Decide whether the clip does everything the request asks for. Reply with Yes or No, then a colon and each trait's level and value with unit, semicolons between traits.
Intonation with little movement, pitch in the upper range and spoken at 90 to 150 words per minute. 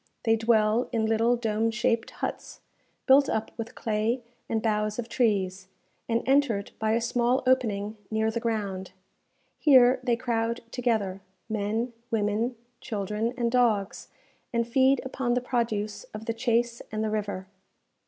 Yes: narrow, 2.2 semitones; high, 225 Hz; average, 145 wpm